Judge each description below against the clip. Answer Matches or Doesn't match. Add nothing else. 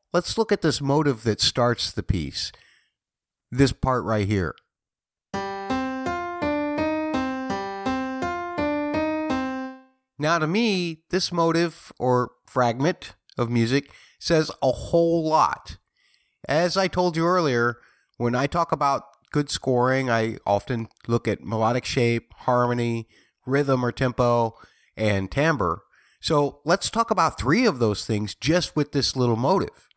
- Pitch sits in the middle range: Matches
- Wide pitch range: Matches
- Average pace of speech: Doesn't match